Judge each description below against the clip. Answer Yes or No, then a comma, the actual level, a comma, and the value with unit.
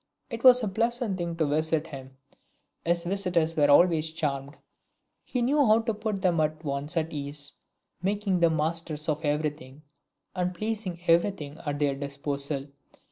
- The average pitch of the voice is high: No, medium, 165 Hz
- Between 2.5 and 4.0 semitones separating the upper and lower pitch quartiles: No, average, 4.7 semitones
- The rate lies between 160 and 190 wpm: Yes, average, 165 wpm